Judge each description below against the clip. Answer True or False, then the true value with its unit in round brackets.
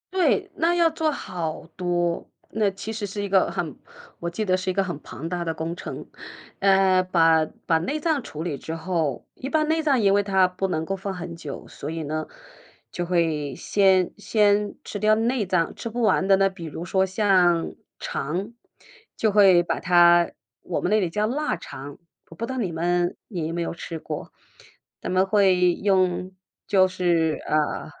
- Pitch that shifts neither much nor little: True (3.4 semitones)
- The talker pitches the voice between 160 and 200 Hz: True (185 Hz)